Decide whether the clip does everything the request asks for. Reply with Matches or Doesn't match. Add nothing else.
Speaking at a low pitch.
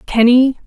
Doesn't match